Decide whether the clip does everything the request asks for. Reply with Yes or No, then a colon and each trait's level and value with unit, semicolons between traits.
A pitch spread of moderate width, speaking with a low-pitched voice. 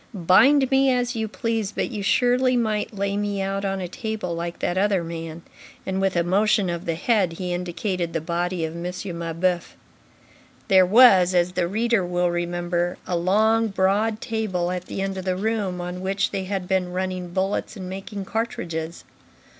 No: average, 3.1 semitones; high, 190 Hz